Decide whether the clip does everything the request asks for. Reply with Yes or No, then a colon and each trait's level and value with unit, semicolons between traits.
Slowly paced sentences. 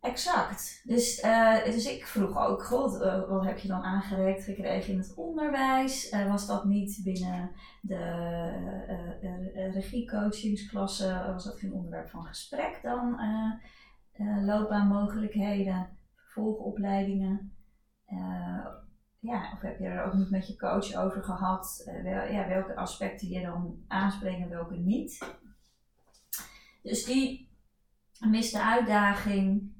Yes: slow, 130 wpm